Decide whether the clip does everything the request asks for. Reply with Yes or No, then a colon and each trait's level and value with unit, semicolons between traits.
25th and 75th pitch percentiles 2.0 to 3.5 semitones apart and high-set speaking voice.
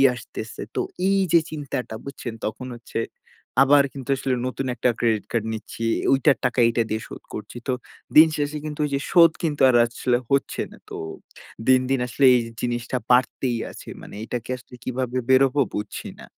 No: average, 2.7 semitones; low, 130 Hz